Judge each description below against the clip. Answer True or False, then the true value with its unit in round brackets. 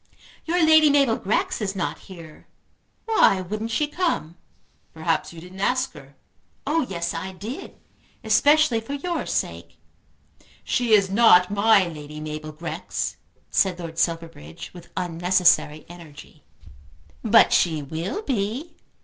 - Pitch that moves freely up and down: True (6.2 semitones)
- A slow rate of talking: True (130 wpm)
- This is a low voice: False (190 Hz)